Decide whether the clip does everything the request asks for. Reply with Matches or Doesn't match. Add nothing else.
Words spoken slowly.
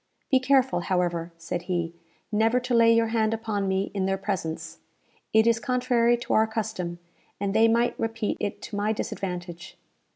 Doesn't match